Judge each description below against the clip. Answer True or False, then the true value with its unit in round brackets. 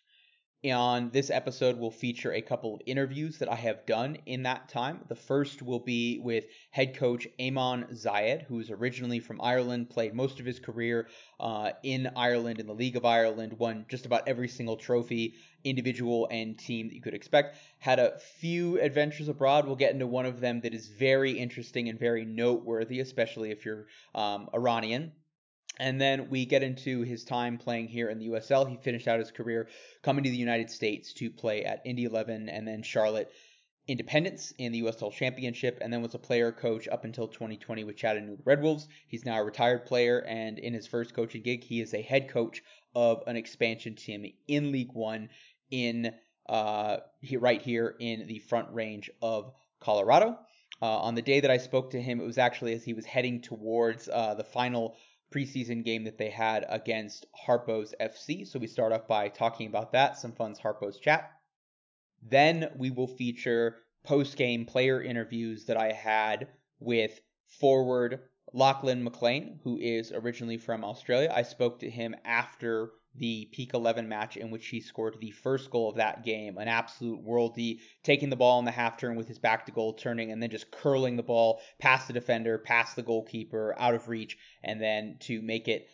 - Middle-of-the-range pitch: False (120 Hz)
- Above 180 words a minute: True (190 wpm)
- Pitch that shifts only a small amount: True (2.2 semitones)